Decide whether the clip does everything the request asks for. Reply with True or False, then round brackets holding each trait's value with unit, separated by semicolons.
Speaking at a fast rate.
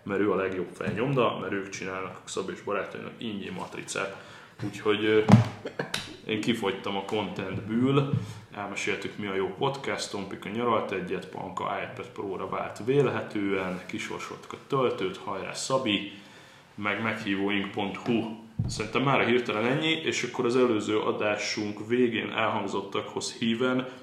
False (130 wpm)